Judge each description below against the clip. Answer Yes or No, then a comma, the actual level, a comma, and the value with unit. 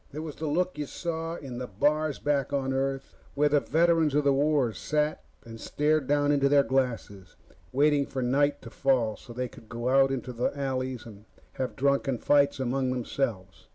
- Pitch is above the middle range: No, low, 135 Hz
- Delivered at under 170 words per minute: No, average, 190 wpm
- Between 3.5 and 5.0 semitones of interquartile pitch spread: No, narrow, 2.6 semitones